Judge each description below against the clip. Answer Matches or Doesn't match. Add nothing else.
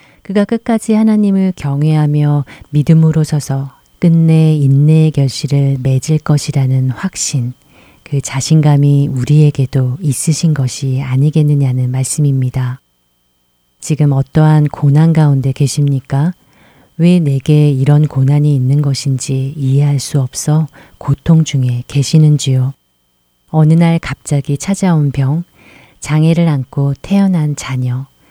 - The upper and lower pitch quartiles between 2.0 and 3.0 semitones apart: Matches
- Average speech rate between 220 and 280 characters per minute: Matches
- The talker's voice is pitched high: Doesn't match